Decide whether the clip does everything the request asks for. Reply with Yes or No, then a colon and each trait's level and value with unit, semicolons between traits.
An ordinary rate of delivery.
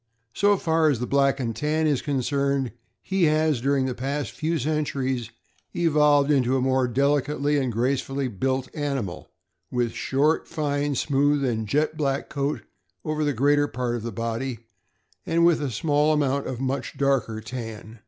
Yes: average, 165 wpm